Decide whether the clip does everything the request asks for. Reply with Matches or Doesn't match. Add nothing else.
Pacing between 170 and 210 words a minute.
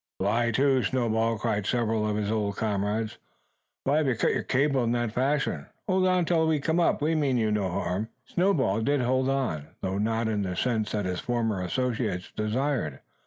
Matches